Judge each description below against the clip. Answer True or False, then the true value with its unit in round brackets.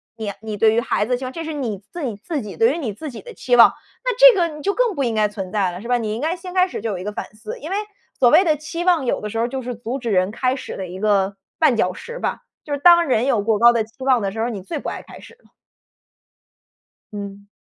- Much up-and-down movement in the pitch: True (6.8 semitones)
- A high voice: True (240 Hz)